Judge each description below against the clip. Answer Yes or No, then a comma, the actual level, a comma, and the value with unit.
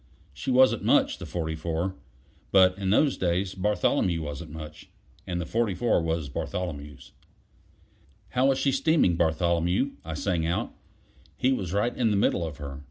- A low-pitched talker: Yes, very low, 90 Hz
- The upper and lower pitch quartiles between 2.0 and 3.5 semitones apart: No, average, 4.6 semitones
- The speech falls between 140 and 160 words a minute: Yes, average, 155 wpm